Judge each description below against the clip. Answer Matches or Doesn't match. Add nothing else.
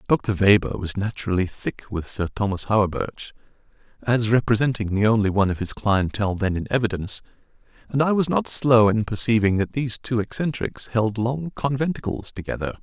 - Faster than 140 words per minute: Matches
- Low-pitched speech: Matches